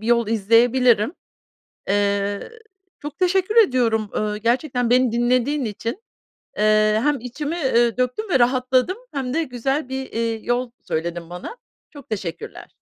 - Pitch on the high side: Yes, high, 245 Hz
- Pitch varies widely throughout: No, average, 3.7 semitones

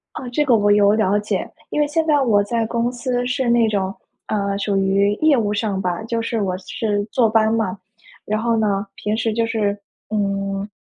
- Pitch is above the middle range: Yes, high, 215 Hz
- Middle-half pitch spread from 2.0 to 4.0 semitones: Yes, average, 2.7 semitones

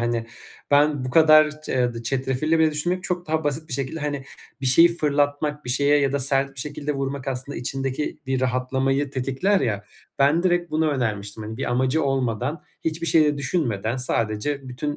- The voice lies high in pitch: No, medium, 140 Hz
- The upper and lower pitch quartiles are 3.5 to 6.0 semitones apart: No, average, 3.1 semitones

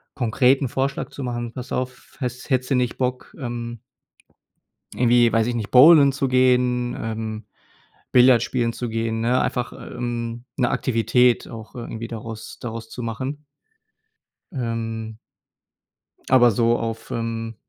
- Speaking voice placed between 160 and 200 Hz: No, low, 120 Hz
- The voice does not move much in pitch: Yes, narrow, 1.9 semitones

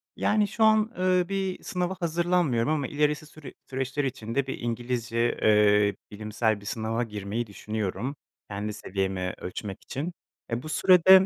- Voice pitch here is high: No, low, 125 Hz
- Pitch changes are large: Yes, wide, 8.3 semitones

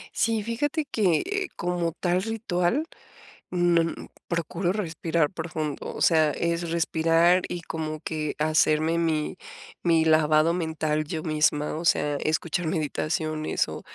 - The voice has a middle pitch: Yes, medium, 165 Hz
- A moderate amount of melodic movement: No, narrow, 2.2 semitones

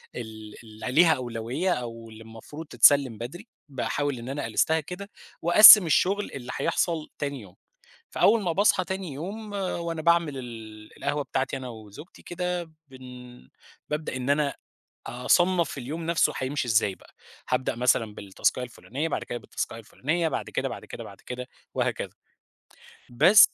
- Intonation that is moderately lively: No, wide, 5.8 semitones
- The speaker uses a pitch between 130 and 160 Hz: Yes, medium, 140 Hz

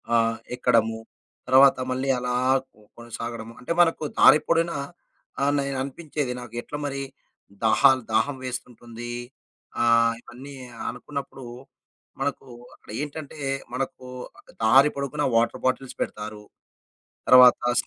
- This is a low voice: Yes, low, 130 Hz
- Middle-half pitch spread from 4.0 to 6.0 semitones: No, average, 3.1 semitones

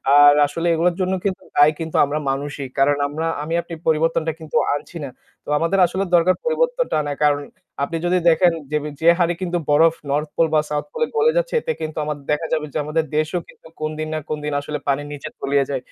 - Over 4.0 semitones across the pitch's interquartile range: No, average, 2.9 semitones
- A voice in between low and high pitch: Yes, medium, 155 Hz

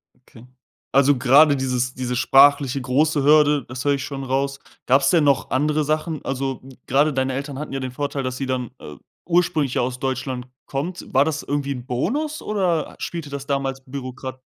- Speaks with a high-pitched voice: No, low, 135 Hz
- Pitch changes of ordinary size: No, narrow, 2.2 semitones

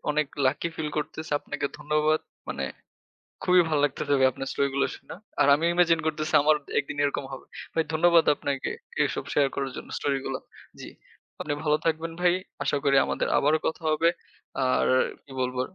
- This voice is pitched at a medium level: Yes, medium, 150 Hz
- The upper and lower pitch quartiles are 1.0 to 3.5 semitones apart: Yes, narrow, 2.4 semitones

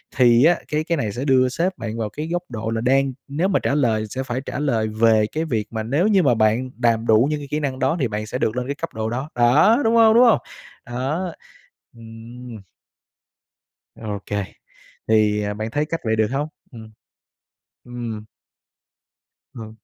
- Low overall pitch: Yes, low, 125 Hz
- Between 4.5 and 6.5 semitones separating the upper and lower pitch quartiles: Yes, average, 4.9 semitones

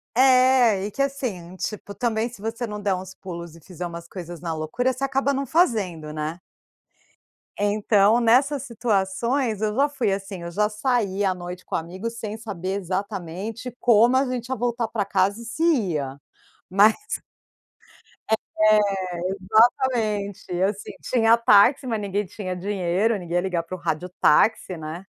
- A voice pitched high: Yes, high, 205 Hz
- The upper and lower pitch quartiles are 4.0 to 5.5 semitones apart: Yes, average, 4.4 semitones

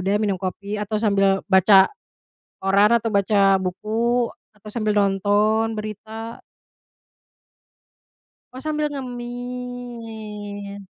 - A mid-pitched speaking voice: No, high, 215 Hz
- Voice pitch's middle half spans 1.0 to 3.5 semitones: Yes, average, 3.2 semitones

